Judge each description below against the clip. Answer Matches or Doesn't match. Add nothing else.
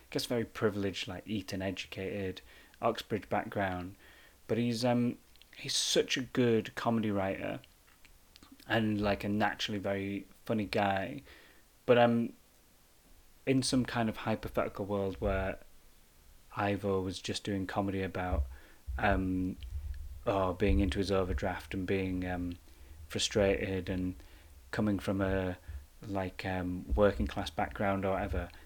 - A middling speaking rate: Doesn't match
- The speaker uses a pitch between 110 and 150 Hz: Doesn't match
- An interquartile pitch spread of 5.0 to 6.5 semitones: Doesn't match